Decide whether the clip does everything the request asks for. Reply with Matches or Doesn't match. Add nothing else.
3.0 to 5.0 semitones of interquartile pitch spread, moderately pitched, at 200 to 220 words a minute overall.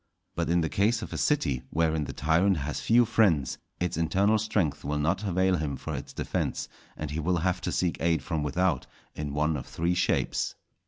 Doesn't match